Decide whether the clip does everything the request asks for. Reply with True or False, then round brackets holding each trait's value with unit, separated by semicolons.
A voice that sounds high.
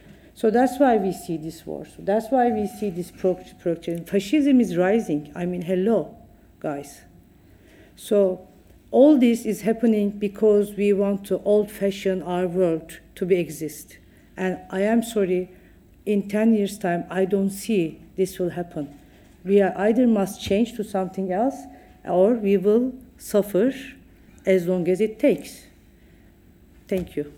True (195 Hz)